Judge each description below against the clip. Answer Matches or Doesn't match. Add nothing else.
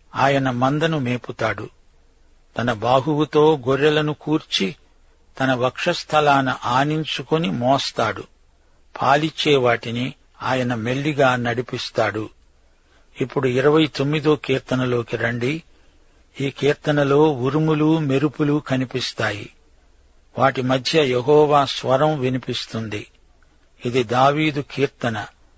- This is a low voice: Matches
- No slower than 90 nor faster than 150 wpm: Doesn't match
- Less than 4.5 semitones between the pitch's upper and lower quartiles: Doesn't match